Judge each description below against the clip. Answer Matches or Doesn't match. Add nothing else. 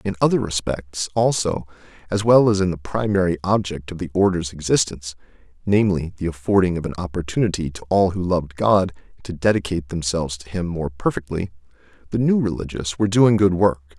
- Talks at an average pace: Matches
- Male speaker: Matches